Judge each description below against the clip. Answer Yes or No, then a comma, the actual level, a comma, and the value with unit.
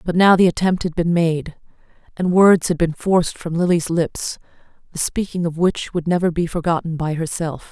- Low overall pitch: No, medium, 170 Hz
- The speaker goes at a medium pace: Yes, average, 195 wpm